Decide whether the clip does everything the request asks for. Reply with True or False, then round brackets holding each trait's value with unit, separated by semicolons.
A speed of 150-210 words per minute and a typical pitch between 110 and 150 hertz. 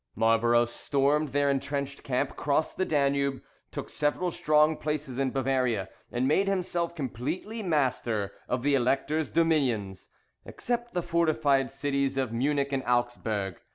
False (135 wpm; 140 Hz)